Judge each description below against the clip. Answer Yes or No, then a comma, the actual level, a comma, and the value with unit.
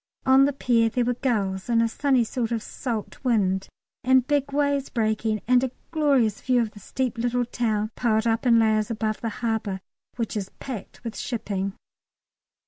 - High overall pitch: Yes, high, 230 Hz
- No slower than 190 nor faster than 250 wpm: No, average, 180 wpm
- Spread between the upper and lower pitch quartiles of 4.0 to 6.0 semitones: No, average, 2.8 semitones